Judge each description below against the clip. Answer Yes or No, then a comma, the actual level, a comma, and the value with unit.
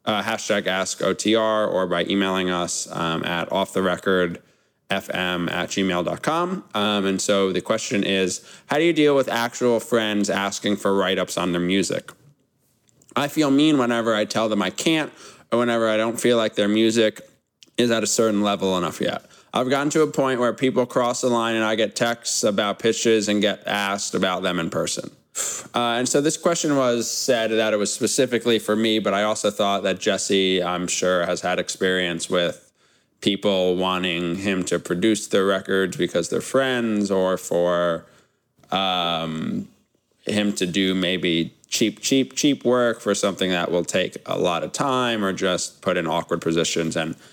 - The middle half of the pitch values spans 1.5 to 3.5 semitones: No, average, 4.2 semitones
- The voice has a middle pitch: No, low, 105 Hz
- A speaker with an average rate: Yes, average, 185 wpm